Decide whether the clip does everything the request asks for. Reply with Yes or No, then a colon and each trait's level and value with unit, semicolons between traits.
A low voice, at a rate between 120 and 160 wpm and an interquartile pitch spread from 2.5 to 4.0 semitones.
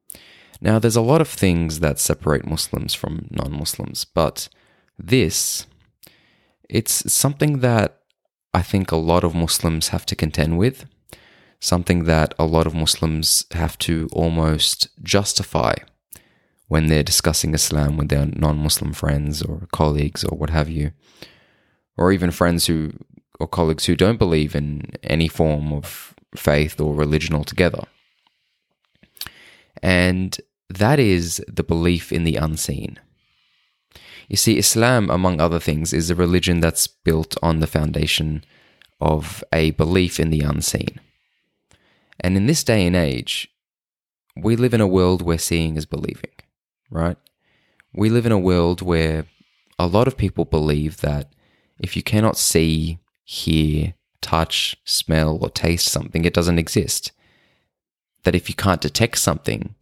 Yes: very low, 85 Hz; average, 140 wpm; average, 2.9 semitones